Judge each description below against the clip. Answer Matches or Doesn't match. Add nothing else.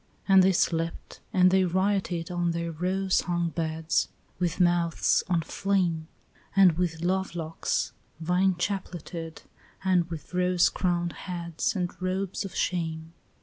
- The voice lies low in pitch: Doesn't match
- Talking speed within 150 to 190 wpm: Doesn't match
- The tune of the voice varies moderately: Doesn't match